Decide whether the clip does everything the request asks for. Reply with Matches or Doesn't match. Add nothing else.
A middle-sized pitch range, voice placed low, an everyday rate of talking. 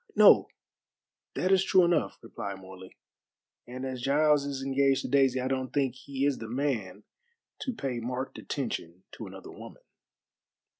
Matches